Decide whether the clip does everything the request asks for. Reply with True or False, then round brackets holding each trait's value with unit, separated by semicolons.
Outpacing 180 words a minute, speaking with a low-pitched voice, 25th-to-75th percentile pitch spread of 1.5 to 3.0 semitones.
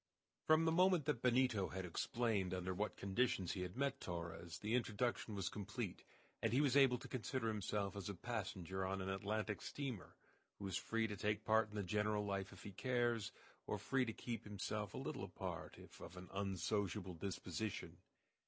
False (190 wpm; 105 Hz; 4.0 semitones)